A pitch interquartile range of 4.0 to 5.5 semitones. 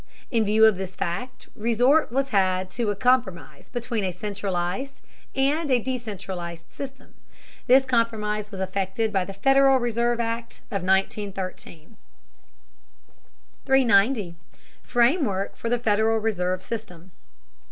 Yes: average, 4.4 semitones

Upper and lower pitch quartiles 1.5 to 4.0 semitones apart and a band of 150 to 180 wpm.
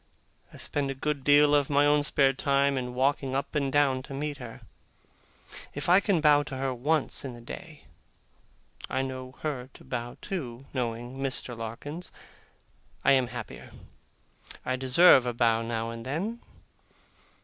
Yes: average, 2.8 semitones; average, 160 wpm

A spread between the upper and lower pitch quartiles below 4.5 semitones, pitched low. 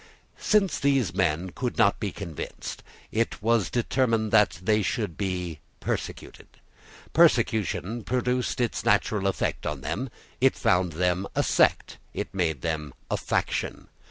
No: average, 4.9 semitones; low, 105 Hz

